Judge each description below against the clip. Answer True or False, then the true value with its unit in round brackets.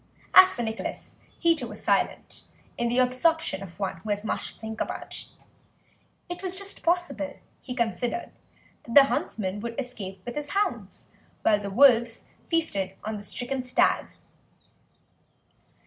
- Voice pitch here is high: True (245 Hz)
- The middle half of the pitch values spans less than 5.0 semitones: False (5.6 semitones)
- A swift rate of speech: False (150 wpm)